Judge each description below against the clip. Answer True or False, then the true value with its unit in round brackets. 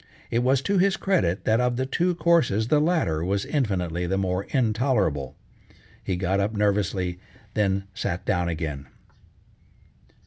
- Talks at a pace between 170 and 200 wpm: False (145 wpm)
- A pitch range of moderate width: False (6.5 semitones)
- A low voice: True (100 Hz)